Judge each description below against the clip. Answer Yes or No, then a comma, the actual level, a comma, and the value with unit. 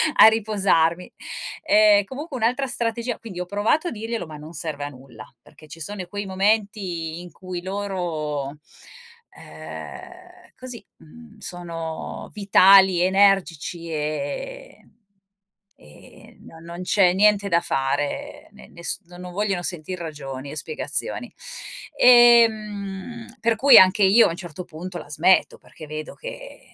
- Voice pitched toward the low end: No, medium, 185 Hz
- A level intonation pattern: No, average, 4.7 semitones